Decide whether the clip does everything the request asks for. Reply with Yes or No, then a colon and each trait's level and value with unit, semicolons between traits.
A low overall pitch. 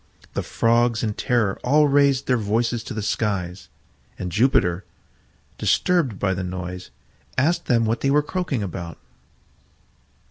Yes: low, 115 Hz